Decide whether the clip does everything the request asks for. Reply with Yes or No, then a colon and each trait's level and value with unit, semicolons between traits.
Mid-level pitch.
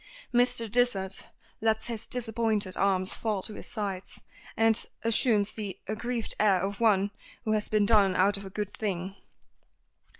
No: high, 210 Hz